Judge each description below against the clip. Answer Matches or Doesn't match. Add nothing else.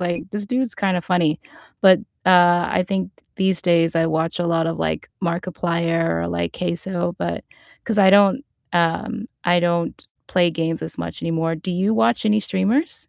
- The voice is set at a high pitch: Doesn't match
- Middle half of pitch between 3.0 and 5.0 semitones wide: Doesn't match